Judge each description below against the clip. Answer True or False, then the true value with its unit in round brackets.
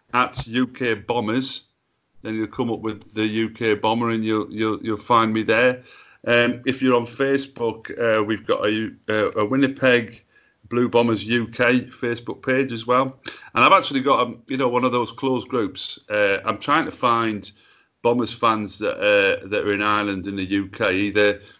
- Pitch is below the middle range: True (115 Hz)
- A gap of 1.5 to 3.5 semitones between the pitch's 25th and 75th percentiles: True (2.7 semitones)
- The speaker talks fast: False (185 wpm)